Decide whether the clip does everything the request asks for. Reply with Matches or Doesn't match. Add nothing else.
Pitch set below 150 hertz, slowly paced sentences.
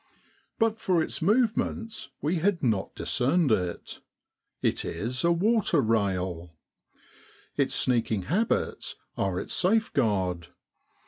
Matches